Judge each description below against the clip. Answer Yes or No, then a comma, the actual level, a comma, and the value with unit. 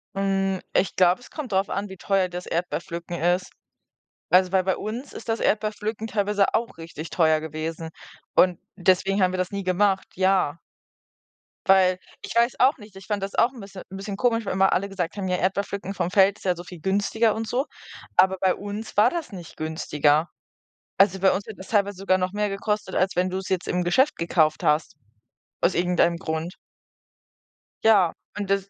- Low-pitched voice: No, high, 190 Hz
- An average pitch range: No, narrow, 2.3 semitones